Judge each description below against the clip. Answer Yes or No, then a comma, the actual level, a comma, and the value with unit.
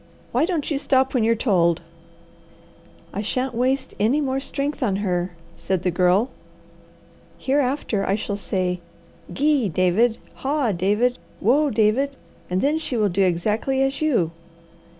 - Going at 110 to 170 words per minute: Yes, average, 145 wpm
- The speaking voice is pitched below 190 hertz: No, high, 230 Hz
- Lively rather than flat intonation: Yes, wide, 6.0 semitones